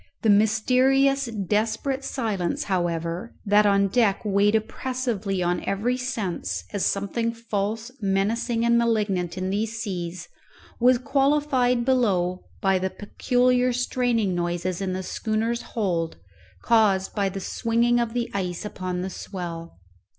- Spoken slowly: Yes, slow, 130 wpm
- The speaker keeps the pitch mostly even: No, average, 4.1 semitones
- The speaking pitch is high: Yes, high, 210 Hz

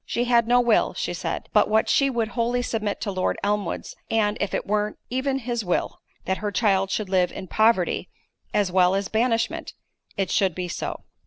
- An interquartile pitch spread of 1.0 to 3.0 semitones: No, average, 3.4 semitones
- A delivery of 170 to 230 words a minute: Yes, average, 195 wpm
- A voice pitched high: Yes, high, 210 Hz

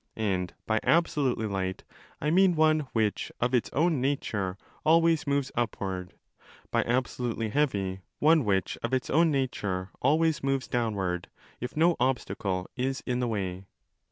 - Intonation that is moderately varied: No, wide, 6.8 semitones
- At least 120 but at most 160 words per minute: Yes, average, 145 wpm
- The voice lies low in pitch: Yes, low, 125 Hz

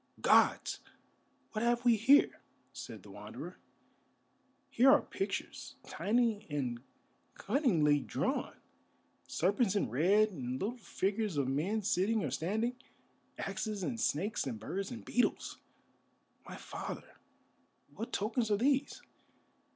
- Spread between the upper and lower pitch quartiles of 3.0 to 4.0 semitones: No, average, 5.1 semitones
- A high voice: Yes, high, 210 Hz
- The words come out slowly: Yes, slow, 120 wpm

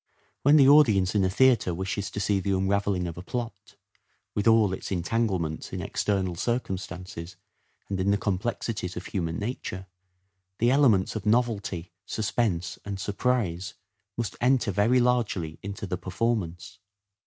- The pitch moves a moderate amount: Yes, average, 4.0 semitones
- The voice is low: Yes, low, 100 Hz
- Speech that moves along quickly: No, average, 150 wpm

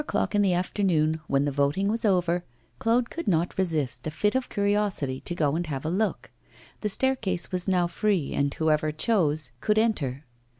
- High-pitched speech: No, medium, 175 Hz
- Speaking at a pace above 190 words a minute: Yes, average, 200 wpm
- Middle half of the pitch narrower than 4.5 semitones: No, average, 5.2 semitones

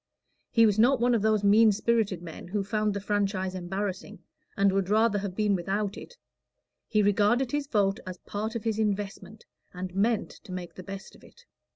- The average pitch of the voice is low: No, high, 205 Hz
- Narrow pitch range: Yes, narrow, 2.2 semitones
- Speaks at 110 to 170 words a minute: No, average, 195 wpm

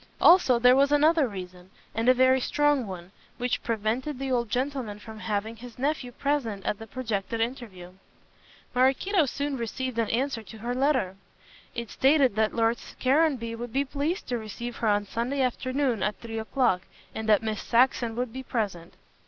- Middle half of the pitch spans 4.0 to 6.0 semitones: No, average, 3.4 semitones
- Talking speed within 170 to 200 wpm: Yes, average, 175 wpm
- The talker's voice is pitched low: No, high, 240 Hz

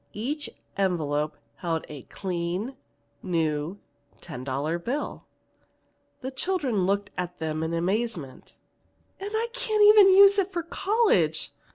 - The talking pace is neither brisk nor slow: No, slow, 120 wpm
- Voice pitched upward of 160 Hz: Yes, high, 190 Hz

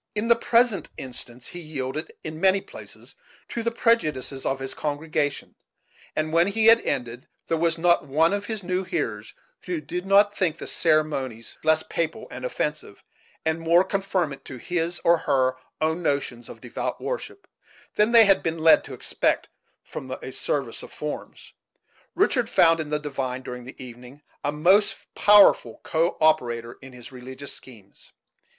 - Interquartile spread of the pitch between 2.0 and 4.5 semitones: No, wide, 5.4 semitones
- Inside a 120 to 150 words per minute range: No, average, 165 wpm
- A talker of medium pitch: Yes, medium, 155 Hz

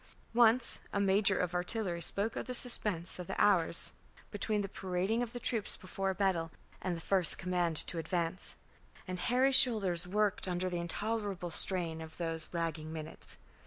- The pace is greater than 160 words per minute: Yes, average, 170 wpm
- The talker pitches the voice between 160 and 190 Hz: Yes, medium, 185 Hz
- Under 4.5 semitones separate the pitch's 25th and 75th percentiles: Yes, average, 3.5 semitones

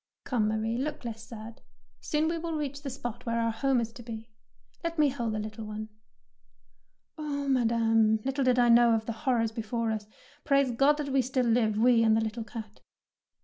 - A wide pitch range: No, average, 3.4 semitones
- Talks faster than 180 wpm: Yes, average, 200 wpm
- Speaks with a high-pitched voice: Yes, high, 235 Hz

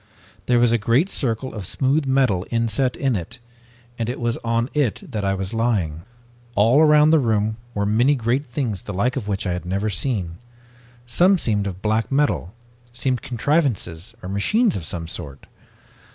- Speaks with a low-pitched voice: Yes, low, 115 Hz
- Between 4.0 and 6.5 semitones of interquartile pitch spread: Yes, average, 4.9 semitones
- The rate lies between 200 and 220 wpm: No, average, 180 wpm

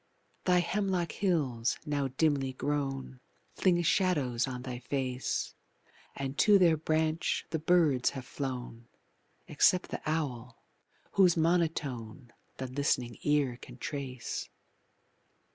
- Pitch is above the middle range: No, medium, 140 Hz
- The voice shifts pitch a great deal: No, average, 4.4 semitones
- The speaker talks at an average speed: No, slow, 110 wpm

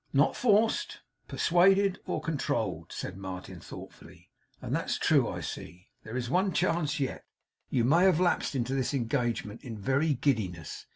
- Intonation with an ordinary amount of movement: No, wide, 7.1 semitones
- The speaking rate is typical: Yes, average, 155 wpm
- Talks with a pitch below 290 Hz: Yes, low, 135 Hz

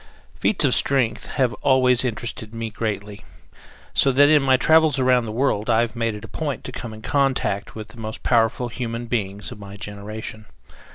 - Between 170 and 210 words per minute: Yes, average, 190 wpm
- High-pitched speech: No, low, 115 Hz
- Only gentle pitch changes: No, average, 3.2 semitones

